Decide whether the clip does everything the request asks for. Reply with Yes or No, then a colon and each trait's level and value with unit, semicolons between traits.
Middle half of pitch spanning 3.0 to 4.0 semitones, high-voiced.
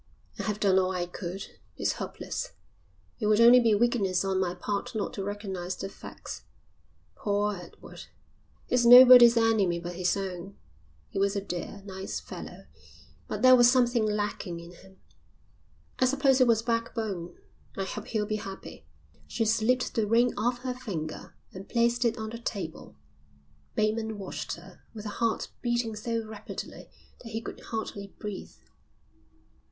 Yes: average, 3.3 semitones; high, 210 Hz